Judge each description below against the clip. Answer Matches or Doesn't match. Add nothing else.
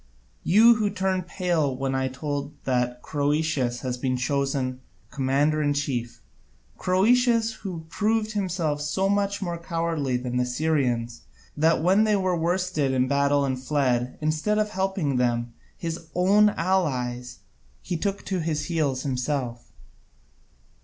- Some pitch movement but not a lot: Doesn't match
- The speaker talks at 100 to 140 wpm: Matches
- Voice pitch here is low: Doesn't match